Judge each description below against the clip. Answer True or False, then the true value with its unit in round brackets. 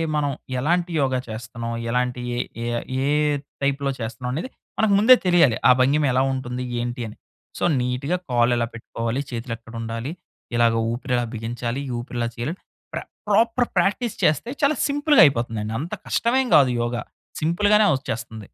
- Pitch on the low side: True (125 Hz)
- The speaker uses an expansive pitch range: True (6.4 semitones)